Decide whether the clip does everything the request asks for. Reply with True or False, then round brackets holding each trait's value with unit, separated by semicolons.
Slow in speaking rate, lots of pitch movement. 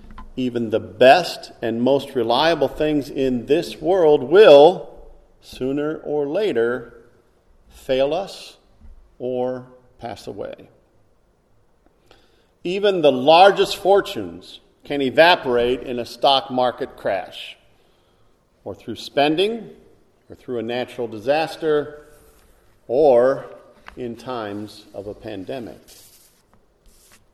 False (95 wpm; 3.8 semitones)